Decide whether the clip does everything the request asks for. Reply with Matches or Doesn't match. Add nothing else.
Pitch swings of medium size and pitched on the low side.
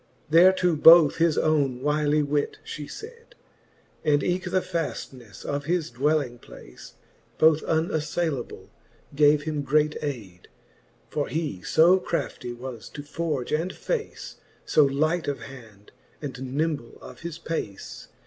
Doesn't match